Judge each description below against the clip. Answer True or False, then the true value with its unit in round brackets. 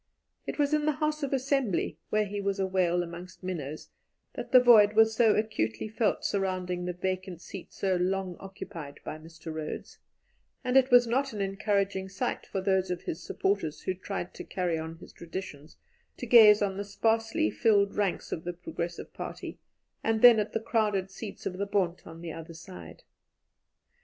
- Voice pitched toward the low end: False (195 Hz)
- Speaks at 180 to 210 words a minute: True (185 wpm)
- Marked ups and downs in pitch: False (3.7 semitones)